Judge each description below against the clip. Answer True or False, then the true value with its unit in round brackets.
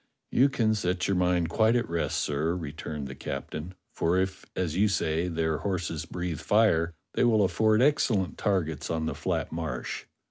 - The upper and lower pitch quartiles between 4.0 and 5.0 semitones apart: True (4.3 semitones)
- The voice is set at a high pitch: False (90 Hz)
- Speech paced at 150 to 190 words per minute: True (175 wpm)